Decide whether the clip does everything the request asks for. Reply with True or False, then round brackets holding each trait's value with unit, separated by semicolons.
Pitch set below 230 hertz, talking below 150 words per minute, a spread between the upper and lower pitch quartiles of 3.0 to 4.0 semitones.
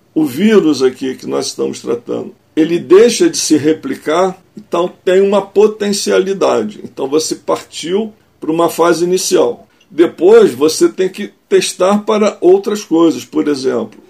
False (190 Hz; 140 wpm; 5.3 semitones)